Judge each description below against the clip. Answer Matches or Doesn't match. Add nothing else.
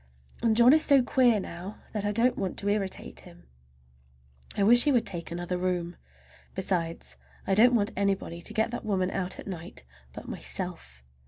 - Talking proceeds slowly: Doesn't match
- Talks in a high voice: Matches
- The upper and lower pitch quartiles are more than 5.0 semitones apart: Doesn't match